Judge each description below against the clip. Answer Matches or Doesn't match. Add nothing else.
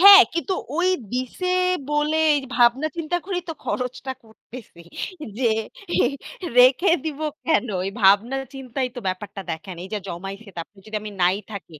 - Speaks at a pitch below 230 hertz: Doesn't match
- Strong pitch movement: Matches